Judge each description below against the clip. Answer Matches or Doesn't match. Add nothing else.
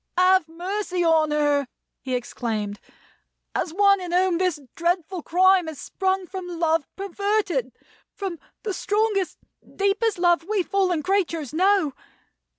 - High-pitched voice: Matches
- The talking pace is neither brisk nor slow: Doesn't match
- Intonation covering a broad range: Doesn't match